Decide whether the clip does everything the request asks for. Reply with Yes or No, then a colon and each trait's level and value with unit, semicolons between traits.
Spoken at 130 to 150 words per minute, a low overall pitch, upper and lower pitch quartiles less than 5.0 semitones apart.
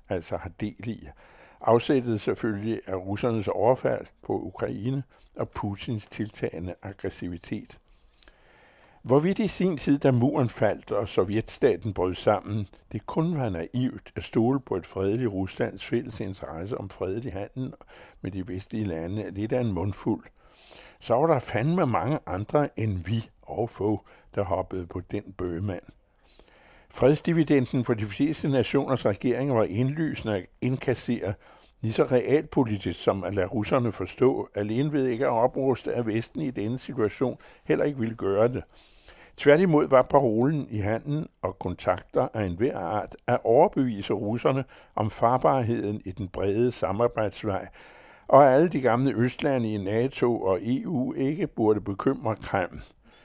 Yes: slow, 145 wpm; low, 115 Hz; average, 4.6 semitones